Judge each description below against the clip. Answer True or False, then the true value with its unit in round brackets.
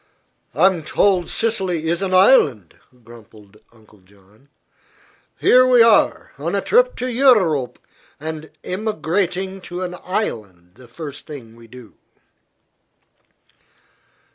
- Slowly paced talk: True (115 wpm)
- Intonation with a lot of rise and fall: True (8.8 semitones)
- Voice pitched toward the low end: False (160 Hz)